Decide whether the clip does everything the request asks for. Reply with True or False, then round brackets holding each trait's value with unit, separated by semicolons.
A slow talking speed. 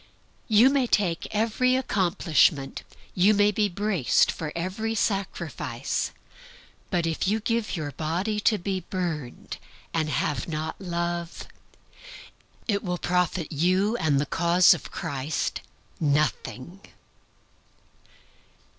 True (110 wpm)